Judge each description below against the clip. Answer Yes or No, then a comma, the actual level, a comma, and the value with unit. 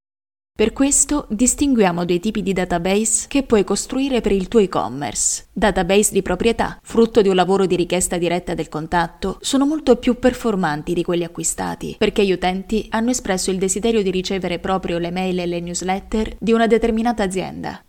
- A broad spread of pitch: No, average, 4.2 semitones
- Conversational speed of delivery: No, fast, 175 wpm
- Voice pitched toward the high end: Yes, high, 195 Hz